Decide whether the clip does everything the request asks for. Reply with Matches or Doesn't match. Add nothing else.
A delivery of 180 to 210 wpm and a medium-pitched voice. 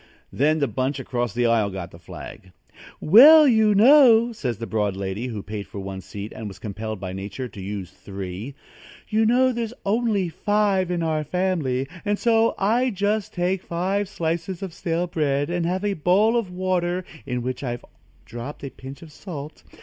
Matches